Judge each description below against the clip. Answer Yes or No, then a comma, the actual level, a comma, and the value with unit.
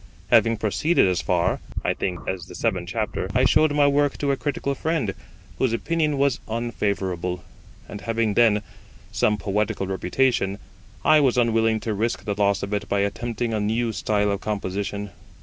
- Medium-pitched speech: No, low, 110 Hz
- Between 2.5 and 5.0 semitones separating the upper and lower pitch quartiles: Yes, average, 3.4 semitones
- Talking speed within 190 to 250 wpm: No, average, 170 wpm